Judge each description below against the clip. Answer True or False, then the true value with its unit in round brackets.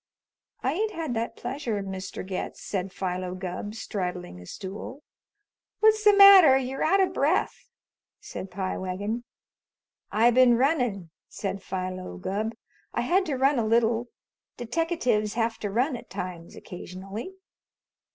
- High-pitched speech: True (225 Hz)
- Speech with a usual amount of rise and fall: False (6.1 semitones)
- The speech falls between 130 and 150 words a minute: True (140 wpm)